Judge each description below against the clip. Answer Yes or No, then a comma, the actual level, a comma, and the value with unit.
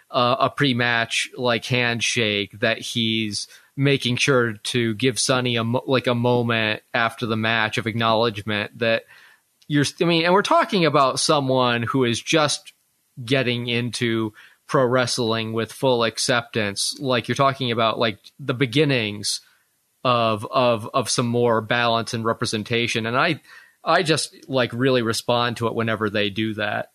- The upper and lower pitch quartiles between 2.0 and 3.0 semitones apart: Yes, narrow, 2.4 semitones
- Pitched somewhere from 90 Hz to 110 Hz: No, low, 120 Hz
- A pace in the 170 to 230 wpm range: No, average, 150 wpm